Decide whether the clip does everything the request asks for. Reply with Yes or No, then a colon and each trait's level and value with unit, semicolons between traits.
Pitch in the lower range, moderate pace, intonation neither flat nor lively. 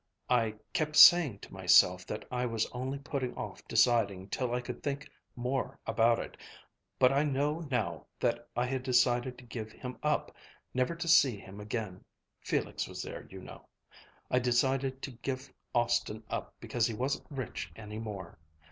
Yes: low, 125 Hz; average, 170 wpm; average, 3.0 semitones